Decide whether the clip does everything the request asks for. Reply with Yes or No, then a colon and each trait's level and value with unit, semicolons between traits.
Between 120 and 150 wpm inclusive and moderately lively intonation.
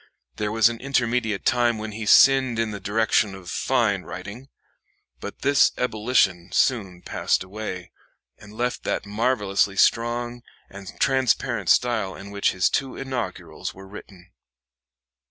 Yes: slow, 135 wpm; average, 3.7 semitones